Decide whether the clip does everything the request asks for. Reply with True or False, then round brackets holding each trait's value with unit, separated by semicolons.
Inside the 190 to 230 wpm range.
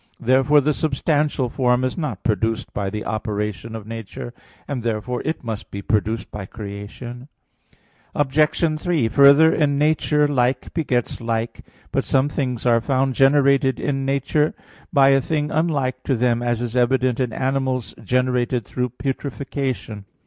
False (150 wpm)